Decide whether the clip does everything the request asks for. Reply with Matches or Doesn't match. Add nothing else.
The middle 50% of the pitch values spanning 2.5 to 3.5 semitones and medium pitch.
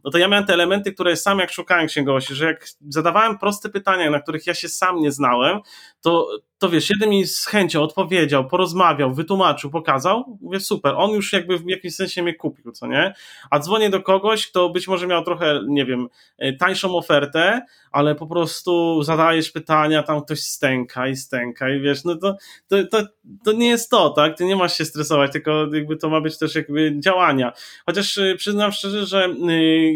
Doesn't match